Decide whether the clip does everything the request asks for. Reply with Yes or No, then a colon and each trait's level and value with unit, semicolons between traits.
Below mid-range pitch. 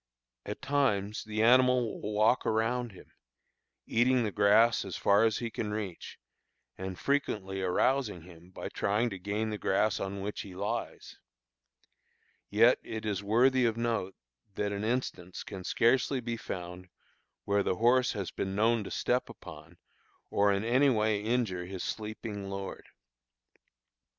Yes: low, 105 Hz